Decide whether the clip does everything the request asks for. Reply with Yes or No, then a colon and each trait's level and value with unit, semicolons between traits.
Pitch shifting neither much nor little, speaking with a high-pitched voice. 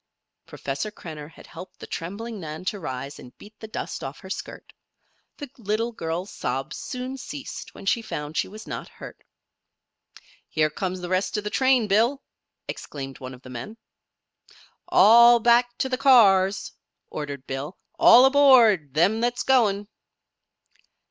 No: wide, 7.4 semitones; high, 205 Hz